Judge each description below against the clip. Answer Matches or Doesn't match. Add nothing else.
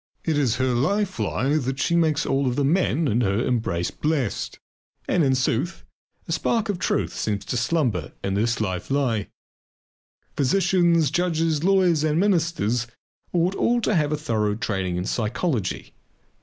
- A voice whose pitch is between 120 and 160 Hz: Matches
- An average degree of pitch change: Doesn't match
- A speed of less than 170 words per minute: Matches